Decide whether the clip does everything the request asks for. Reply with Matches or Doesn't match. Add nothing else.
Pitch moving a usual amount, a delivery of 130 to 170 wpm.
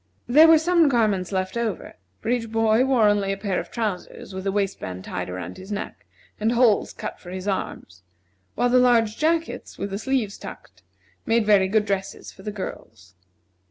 Doesn't match